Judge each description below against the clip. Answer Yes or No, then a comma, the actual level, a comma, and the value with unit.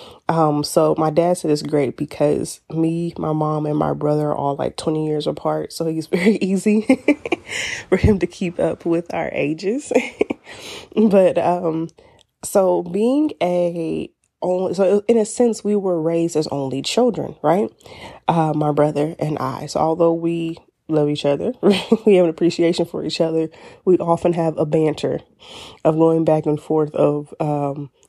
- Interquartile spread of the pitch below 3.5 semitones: Yes, average, 3.1 semitones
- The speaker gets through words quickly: No, average, 170 wpm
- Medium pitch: Yes, medium, 165 Hz